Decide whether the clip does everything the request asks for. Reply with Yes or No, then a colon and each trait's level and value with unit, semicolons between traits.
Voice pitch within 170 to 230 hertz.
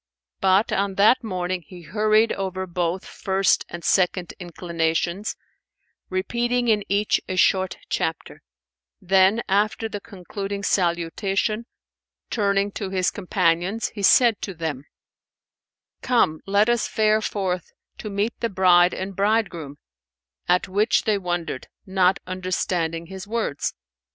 Yes: high, 190 Hz